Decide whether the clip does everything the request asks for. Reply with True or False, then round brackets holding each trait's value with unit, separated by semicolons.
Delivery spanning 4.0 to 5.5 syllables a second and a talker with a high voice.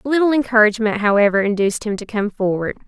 False (7.1 syllables/s; 220 Hz)